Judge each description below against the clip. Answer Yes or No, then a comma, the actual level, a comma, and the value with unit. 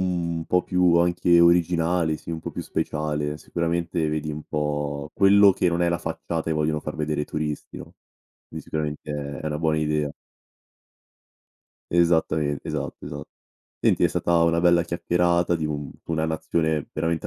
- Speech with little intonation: Yes, narrow, 2.1 semitones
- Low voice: Yes, very low, 80 Hz